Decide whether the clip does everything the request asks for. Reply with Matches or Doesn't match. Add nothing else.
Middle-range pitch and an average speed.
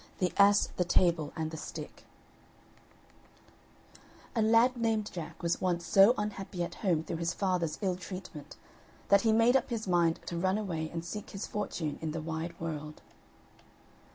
Matches